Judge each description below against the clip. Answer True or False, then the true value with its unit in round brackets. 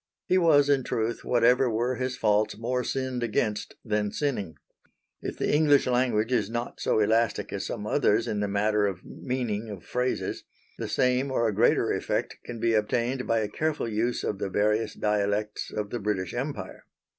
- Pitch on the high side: False (115 Hz)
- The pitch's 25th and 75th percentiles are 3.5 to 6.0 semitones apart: False (3.1 semitones)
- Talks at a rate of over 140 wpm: True (180 wpm)